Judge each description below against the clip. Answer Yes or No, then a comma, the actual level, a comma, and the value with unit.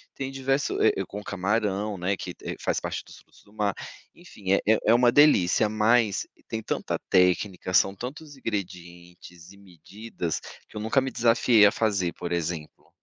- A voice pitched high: No, low, 105 Hz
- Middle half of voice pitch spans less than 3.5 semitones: No, average, 4.0 semitones